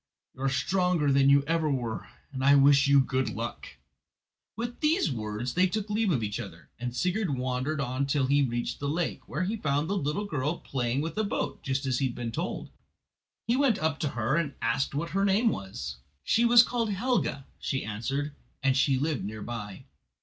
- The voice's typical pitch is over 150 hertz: No, medium, 140 Hz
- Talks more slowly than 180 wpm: No, fast, 205 wpm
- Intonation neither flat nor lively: No, wide, 6.2 semitones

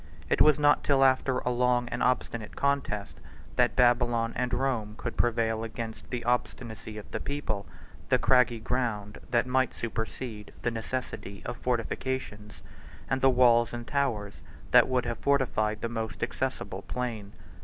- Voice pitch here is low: Yes, low, 120 Hz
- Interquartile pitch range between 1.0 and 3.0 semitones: Yes, narrow, 2.5 semitones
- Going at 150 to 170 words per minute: Yes, average, 155 wpm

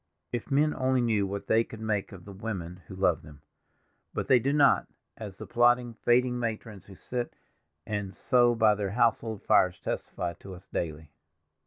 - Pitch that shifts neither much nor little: Yes, average, 4.0 semitones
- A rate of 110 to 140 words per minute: No, average, 175 wpm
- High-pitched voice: No, low, 110 Hz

